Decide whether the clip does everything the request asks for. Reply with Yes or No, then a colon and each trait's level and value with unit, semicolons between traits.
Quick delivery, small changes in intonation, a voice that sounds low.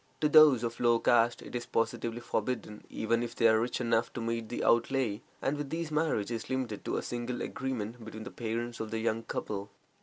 Yes: fast, 215 wpm; narrow, 1.9 semitones; low, 115 Hz